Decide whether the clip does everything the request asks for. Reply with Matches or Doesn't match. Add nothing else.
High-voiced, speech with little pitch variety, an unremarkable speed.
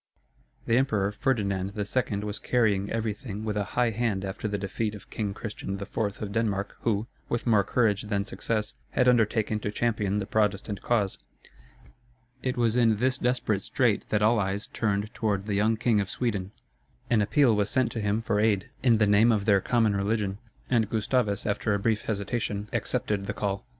Doesn't match